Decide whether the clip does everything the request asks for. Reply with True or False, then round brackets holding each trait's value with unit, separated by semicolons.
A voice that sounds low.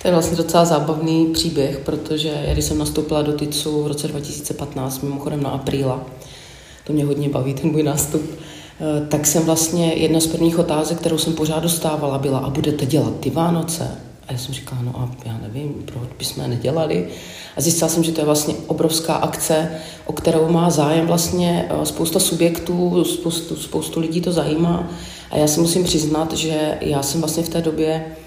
False (155 Hz)